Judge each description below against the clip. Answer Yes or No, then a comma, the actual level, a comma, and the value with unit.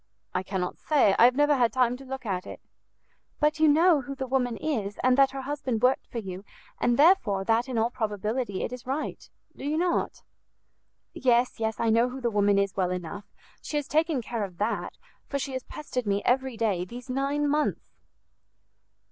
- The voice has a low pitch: No, high, 245 Hz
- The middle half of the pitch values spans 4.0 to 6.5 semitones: Yes, average, 4.7 semitones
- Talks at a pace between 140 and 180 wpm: No, average, 200 wpm